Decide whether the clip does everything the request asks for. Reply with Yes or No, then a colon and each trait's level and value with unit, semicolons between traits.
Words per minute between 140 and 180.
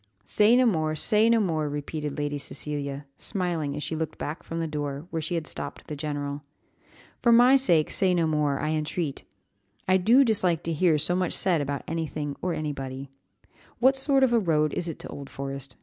No: average, 200 wpm